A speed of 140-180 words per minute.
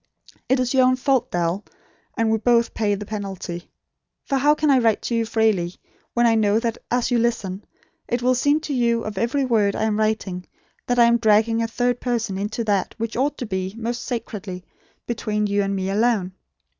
No: fast, 205 wpm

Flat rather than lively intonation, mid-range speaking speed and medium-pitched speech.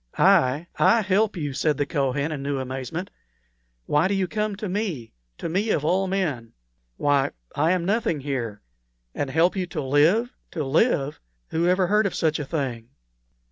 No: wide, 5.5 semitones; average, 180 wpm; medium, 160 Hz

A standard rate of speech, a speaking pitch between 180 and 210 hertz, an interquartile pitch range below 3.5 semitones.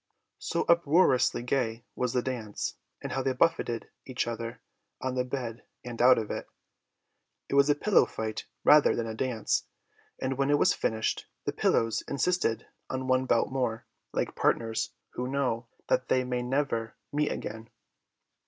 No: average, 160 wpm; low, 125 Hz; average, 2.8 semitones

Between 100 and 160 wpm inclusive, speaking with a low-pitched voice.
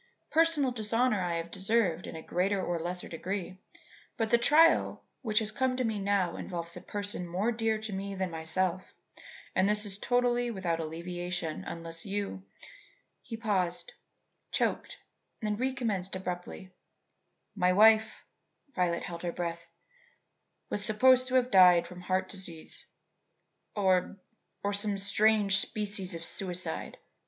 No: average, 140 wpm; high, 195 Hz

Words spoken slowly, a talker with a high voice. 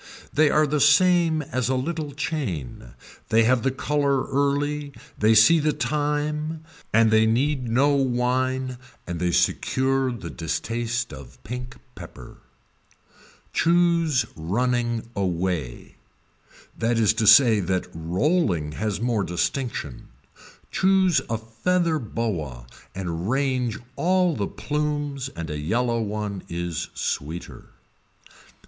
No: slow, 120 wpm; low, 125 Hz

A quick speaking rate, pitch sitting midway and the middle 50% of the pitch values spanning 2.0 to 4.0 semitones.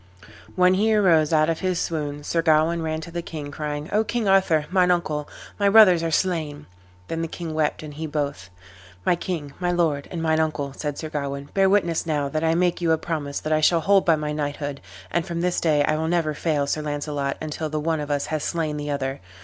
Yes: fast, 230 wpm; medium, 155 Hz; narrow, 2.6 semitones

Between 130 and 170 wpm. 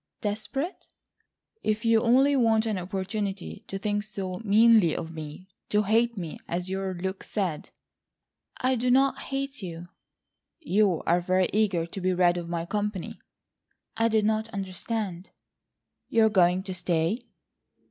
Yes: average, 145 wpm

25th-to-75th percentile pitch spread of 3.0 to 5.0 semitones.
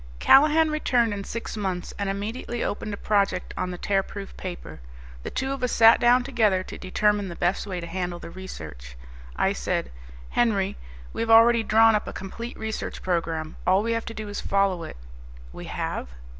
Yes: average, 3.8 semitones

